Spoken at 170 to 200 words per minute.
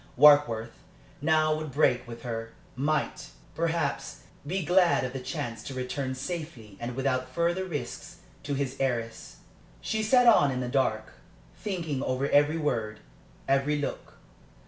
No: average, 145 wpm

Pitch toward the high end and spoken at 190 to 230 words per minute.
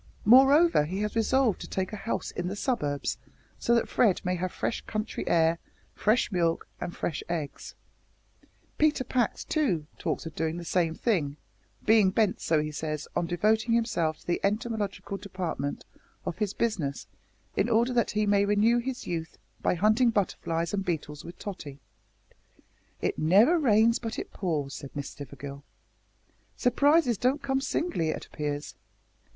No: high, 200 Hz; average, 160 wpm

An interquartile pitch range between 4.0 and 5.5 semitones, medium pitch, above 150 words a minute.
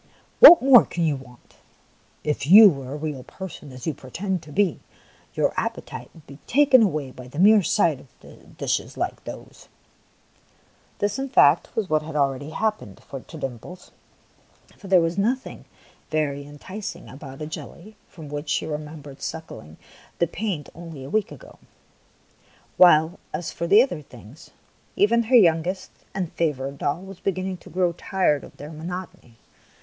Yes: average, 5.1 semitones; medium, 165 Hz; average, 165 wpm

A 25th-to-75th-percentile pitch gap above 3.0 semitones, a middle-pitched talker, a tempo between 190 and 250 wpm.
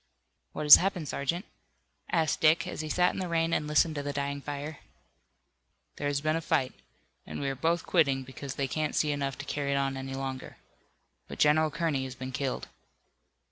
No: narrow, 2.6 semitones; medium, 145 Hz; average, 195 wpm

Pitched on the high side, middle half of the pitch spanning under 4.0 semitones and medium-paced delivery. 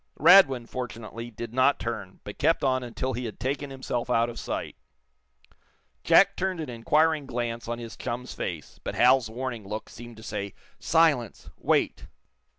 No: low, 120 Hz; average, 2.8 semitones; average, 160 wpm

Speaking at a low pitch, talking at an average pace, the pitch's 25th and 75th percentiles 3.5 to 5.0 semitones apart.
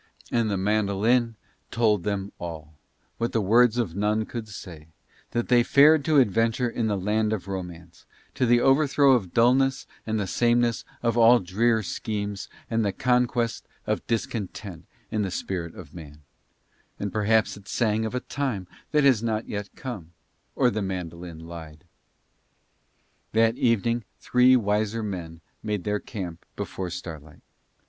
Yes: low, 110 Hz; average, 155 wpm; average, 3.9 semitones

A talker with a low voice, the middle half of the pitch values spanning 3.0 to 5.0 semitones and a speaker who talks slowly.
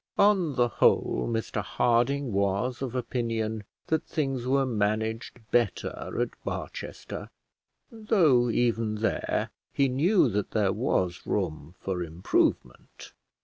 Yes: low, 120 Hz; average, 4.4 semitones; slow, 115 wpm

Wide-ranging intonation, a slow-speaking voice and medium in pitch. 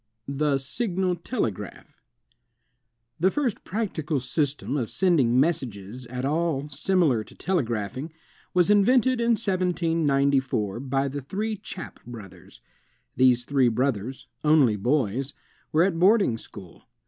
Yes: wide, 6.5 semitones; slow, 115 wpm; medium, 145 Hz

